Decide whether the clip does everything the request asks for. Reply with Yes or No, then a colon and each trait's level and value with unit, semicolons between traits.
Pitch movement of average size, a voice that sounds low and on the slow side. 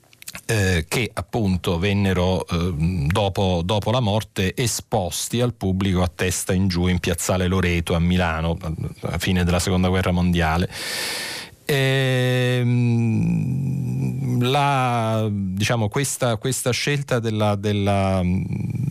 Yes: average, 4.8 semitones; low, 100 Hz; slow, 110 wpm